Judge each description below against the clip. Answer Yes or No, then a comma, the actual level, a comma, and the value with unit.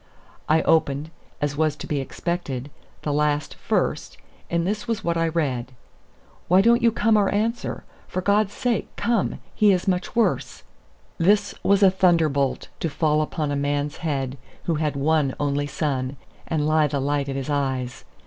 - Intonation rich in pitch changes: No, average, 4.6 semitones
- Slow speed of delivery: No, average, 170 wpm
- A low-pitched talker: No, medium, 155 Hz